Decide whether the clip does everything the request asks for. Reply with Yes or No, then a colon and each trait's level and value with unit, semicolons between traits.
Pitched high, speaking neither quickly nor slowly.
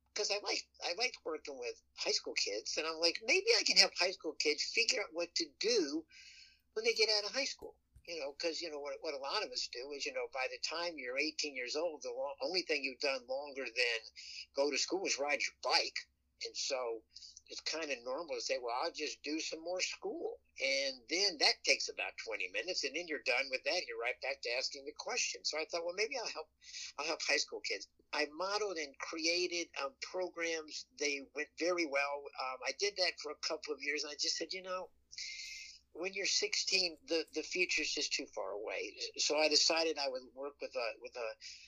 No: very high, 310 Hz; fast, 235 wpm